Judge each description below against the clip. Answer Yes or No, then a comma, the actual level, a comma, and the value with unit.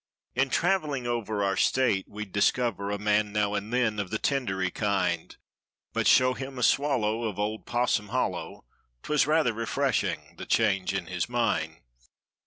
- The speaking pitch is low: Yes, low, 110 Hz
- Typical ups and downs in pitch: Yes, average, 3.7 semitones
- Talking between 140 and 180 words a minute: Yes, average, 160 wpm